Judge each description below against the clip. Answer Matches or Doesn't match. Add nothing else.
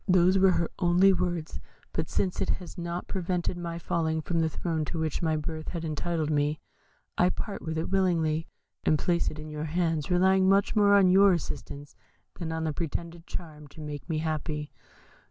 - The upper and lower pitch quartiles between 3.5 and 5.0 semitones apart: Doesn't match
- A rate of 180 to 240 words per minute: Matches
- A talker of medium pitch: Matches